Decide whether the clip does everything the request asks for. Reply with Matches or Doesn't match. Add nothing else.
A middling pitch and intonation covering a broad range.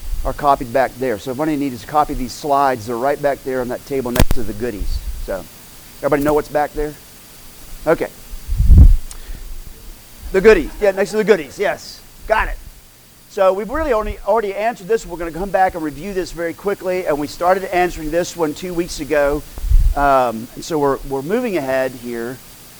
Matches